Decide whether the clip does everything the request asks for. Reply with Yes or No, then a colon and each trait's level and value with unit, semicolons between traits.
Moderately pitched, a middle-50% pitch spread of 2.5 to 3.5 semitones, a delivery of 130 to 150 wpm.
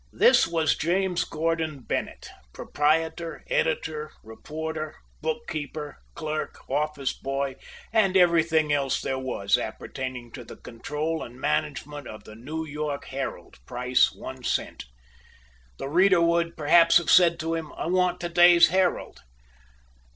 Yes: medium, 155 Hz; average, 3.2 semitones; slow, 135 wpm